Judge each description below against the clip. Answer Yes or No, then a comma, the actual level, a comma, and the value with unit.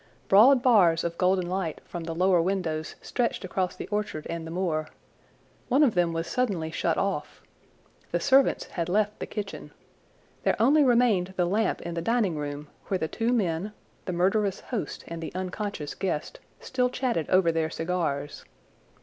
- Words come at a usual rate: Yes, average, 170 wpm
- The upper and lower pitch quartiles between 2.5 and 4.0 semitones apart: No, average, 4.4 semitones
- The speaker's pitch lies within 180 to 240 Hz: Yes, medium, 185 Hz